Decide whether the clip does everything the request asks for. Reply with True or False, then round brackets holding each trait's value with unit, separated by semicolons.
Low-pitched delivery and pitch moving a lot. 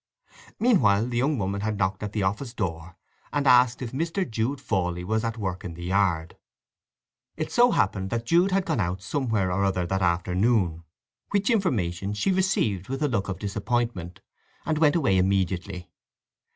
True (105 Hz; 6.2 semitones)